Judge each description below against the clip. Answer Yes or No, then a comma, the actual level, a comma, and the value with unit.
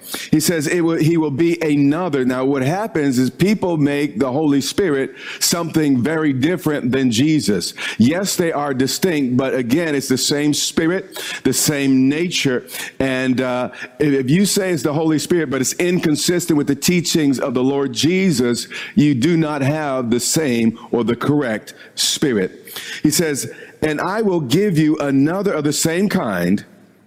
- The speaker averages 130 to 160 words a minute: No, average, 170 wpm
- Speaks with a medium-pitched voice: Yes, medium, 150 Hz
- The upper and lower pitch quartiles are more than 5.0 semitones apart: No, average, 4.2 semitones